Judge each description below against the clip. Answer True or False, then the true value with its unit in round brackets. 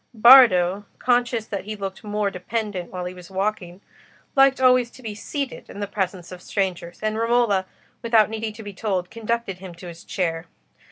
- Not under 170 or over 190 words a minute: True (180 wpm)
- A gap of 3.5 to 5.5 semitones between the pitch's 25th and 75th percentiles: True (3.9 semitones)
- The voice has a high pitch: True (205 Hz)